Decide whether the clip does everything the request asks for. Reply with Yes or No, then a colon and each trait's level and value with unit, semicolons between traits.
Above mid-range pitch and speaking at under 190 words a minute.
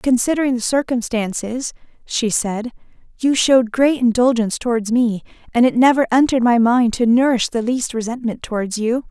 Yes: high, 240 Hz; average, 160 wpm